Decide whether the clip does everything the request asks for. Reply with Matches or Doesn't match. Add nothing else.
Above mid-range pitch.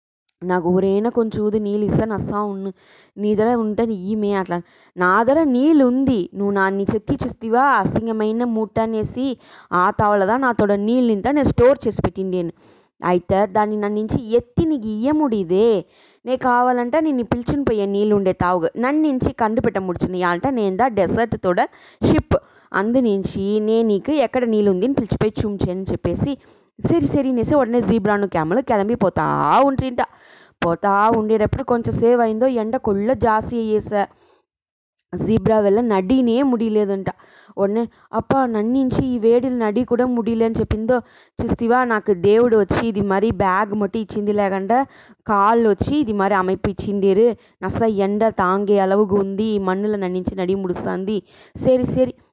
Matches